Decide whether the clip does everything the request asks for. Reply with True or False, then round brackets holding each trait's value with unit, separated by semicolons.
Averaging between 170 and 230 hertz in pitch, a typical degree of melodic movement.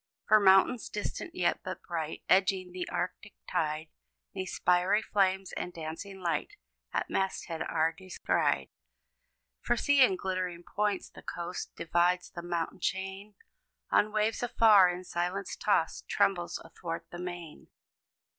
False (185 Hz; 2.1 semitones)